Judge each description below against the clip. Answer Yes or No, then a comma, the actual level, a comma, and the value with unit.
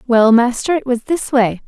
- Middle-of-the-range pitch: No, high, 245 Hz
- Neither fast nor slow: No, fast, 215 wpm